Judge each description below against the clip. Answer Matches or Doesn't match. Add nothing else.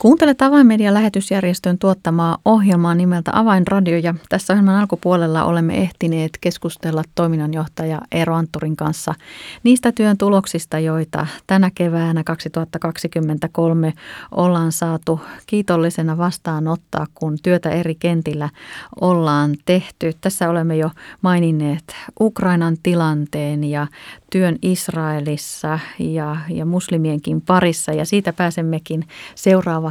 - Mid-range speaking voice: Matches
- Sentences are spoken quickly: Doesn't match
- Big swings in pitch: Doesn't match